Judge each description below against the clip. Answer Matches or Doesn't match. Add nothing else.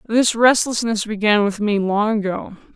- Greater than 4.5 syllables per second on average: Doesn't match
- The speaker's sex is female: Matches